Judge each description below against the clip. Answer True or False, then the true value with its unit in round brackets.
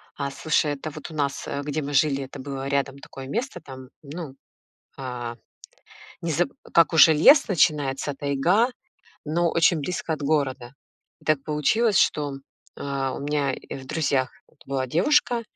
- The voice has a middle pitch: True (145 Hz)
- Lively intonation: False (2.9 semitones)